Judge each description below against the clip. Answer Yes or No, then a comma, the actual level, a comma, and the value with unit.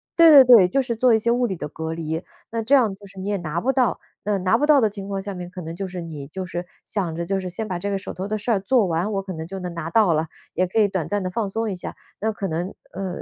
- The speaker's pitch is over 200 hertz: No, high, 195 Hz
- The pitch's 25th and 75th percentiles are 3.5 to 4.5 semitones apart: Yes, average, 3.9 semitones